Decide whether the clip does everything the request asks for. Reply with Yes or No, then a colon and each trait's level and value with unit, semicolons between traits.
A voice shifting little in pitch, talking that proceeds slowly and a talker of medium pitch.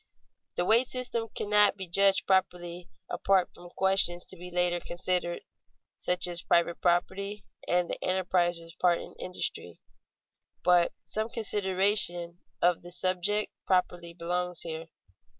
Yes: narrow, 1.8 semitones; slow, 130 wpm; medium, 180 Hz